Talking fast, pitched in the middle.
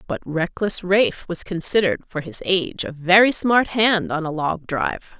No: average, 185 wpm; medium, 180 Hz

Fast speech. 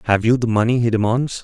Yes: fast, 250 wpm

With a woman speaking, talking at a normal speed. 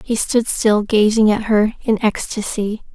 Yes: female; average, 165 wpm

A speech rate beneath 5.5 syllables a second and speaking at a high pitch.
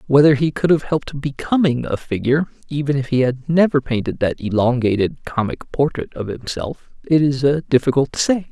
No: 5.3 syllables/s; low, 135 Hz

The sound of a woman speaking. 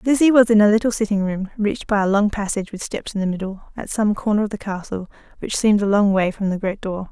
Yes: female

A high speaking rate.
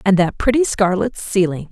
No: average, 175 wpm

